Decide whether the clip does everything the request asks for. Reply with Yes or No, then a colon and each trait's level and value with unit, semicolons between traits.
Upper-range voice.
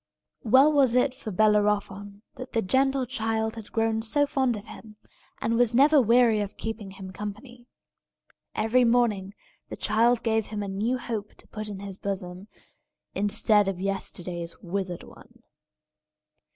Yes: high, 220 Hz